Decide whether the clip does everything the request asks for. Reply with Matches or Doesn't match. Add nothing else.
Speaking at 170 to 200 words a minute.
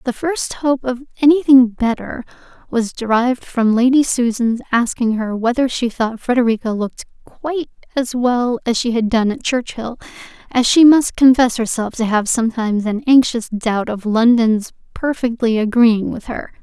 Doesn't match